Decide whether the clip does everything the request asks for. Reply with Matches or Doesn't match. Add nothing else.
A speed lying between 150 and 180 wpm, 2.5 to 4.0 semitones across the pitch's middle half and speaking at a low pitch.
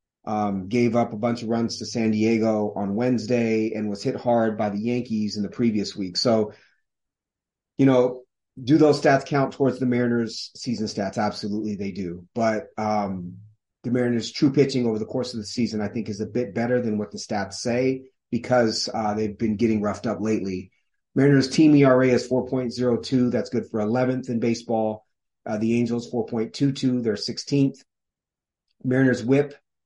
Matches